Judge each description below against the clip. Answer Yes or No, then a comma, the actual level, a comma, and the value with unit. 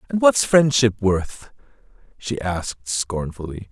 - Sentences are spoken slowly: Yes, slow, 115 wpm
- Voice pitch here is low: Yes, low, 115 Hz